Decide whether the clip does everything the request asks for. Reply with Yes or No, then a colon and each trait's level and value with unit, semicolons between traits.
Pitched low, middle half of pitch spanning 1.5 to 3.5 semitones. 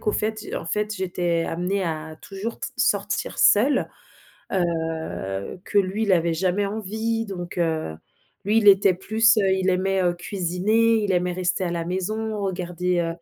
No: high, 190 Hz; average, 3.2 semitones